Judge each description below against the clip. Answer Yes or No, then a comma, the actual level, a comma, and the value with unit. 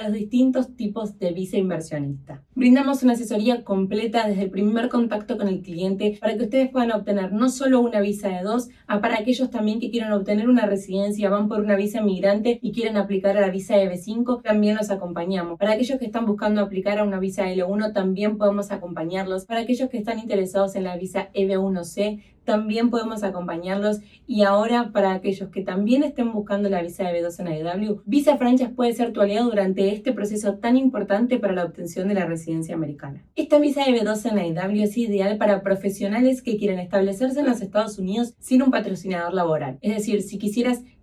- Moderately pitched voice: No, high, 205 Hz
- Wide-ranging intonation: No, average, 3.2 semitones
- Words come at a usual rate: No, fast, 195 wpm